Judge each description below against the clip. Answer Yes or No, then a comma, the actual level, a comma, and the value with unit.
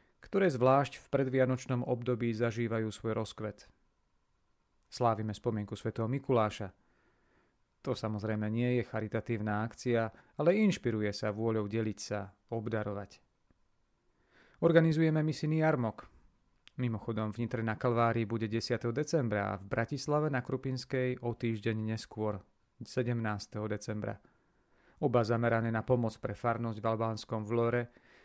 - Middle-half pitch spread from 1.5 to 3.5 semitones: Yes, narrow, 2.6 semitones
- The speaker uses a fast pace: No, average, 115 wpm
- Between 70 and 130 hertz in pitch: Yes, low, 115 Hz